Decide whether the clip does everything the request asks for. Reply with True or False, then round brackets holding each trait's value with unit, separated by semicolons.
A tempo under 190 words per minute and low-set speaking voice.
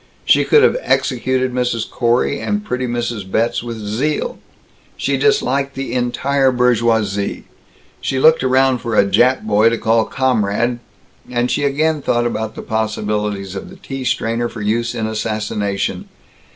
True (150 wpm; 120 Hz)